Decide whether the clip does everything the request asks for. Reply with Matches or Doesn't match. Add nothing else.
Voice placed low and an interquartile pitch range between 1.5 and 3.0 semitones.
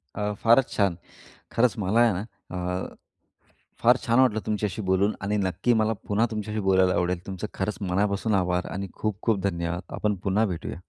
Matches